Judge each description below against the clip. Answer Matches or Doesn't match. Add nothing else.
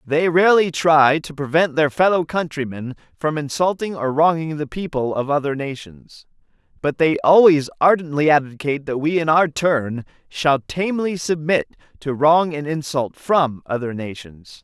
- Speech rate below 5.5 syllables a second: Matches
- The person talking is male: Matches